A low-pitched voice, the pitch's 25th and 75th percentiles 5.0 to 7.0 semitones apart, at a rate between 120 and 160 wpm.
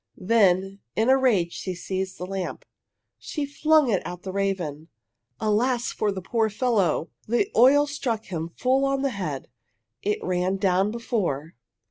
No: high, 200 Hz; wide, 5.4 semitones; average, 155 wpm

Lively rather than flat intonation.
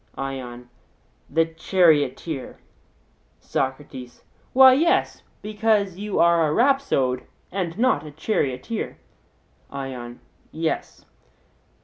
Yes: wide, 7.9 semitones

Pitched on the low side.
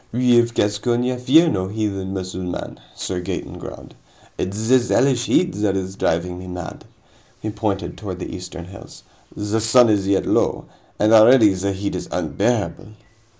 Yes: low, 105 Hz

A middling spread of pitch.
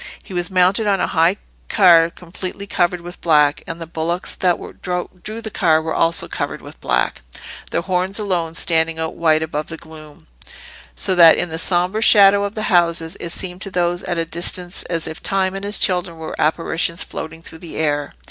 No: narrow, 2.3 semitones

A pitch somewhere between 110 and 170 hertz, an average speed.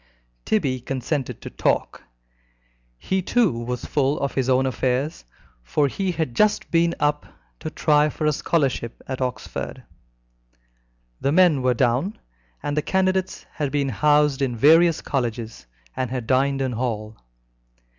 Yes: medium, 140 Hz; average, 145 wpm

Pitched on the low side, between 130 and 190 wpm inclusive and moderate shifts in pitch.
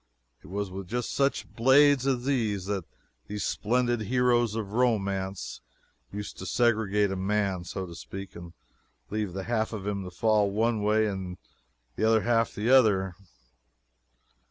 Yes: low, 105 Hz; average, 155 wpm; average, 3.4 semitones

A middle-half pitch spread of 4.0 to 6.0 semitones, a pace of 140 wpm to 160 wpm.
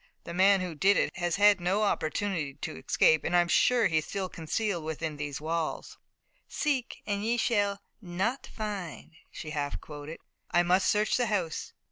No: average, 4.4 semitones; average, 175 wpm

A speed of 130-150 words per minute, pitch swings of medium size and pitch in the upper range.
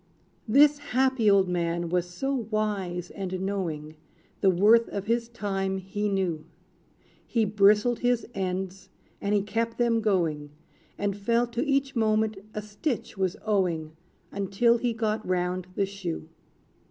Yes: average, 140 wpm; average, 3.8 semitones; high, 200 Hz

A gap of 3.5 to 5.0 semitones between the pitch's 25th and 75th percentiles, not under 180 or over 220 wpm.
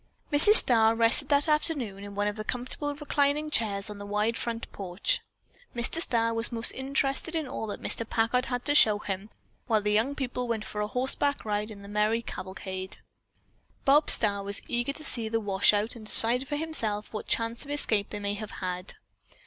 Yes: average, 4.6 semitones; average, 195 wpm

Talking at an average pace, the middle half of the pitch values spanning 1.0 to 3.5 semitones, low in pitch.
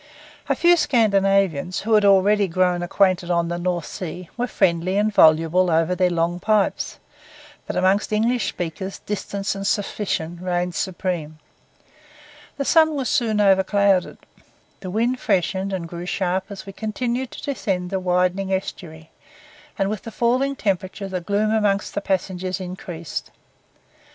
No: average, 145 wpm; average, 2.7 semitones; high, 190 Hz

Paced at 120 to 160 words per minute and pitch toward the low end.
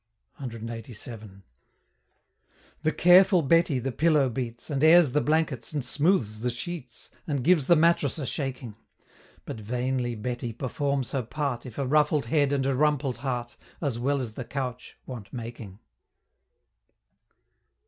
Yes: average, 140 wpm; low, 130 Hz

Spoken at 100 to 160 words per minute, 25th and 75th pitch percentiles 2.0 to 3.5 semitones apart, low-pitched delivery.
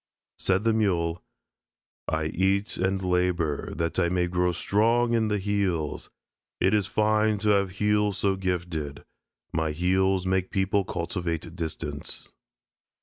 Yes: slow, 135 wpm; average, 3.1 semitones; very low, 95 Hz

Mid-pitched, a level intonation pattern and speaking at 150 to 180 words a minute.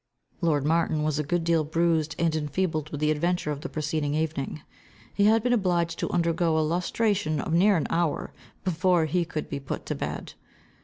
No: medium, 165 Hz; narrow, 2.3 semitones; average, 195 wpm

